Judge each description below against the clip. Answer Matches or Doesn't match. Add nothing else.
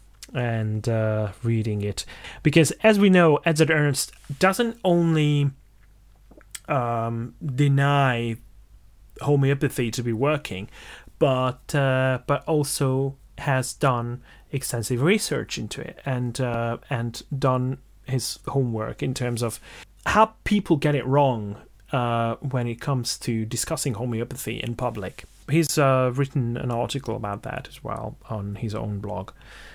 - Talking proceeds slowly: Matches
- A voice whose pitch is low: Matches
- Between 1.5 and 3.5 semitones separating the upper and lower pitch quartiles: Doesn't match